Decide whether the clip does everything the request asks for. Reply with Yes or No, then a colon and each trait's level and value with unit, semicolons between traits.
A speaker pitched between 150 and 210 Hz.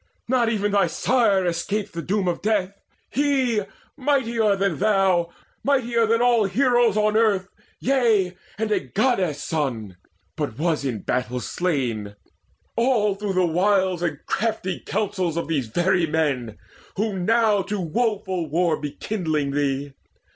Yes: high, 190 Hz